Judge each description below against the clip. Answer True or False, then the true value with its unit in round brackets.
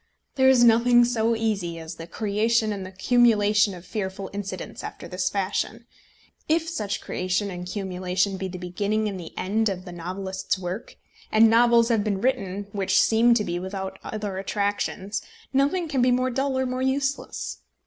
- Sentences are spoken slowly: False (175 wpm)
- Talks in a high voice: True (205 Hz)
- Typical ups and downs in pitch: True (3.8 semitones)